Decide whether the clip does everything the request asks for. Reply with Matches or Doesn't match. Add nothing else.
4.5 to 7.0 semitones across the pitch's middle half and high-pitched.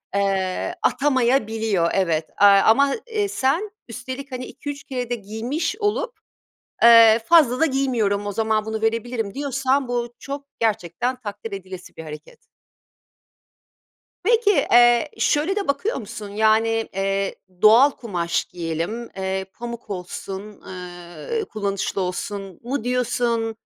Matches